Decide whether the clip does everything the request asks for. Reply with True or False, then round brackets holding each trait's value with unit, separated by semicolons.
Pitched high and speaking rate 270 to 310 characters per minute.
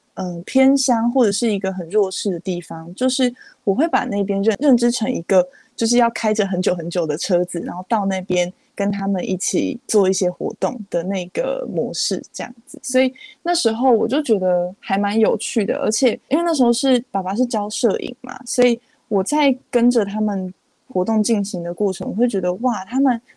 True (220 Hz; 290 characters per minute)